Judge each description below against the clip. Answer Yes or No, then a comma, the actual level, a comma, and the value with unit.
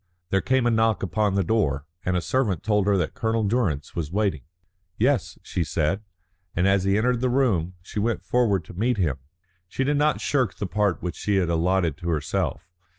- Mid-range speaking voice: No, low, 100 Hz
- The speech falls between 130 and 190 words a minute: No, fast, 205 wpm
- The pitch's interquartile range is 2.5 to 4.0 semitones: No, average, 4.5 semitones